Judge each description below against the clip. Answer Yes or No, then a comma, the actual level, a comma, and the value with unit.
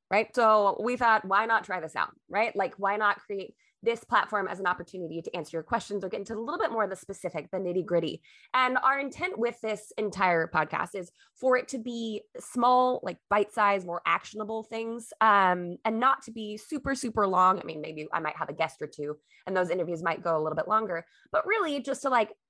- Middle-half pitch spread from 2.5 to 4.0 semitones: No, average, 5.0 semitones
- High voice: Yes, high, 210 Hz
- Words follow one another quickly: Yes, fast, 230 wpm